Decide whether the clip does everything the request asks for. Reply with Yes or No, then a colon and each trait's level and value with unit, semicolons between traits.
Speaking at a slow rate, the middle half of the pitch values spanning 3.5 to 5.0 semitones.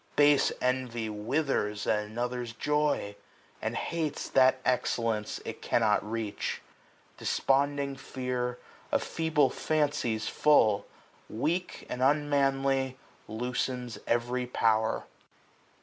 Yes: slow, 100 wpm; average, 3.8 semitones